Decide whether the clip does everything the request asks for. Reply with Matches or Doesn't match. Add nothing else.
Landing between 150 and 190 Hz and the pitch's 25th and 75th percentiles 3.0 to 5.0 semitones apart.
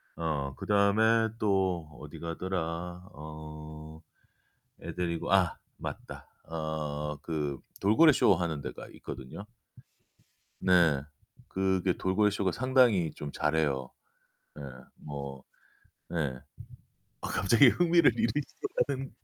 Doesn't match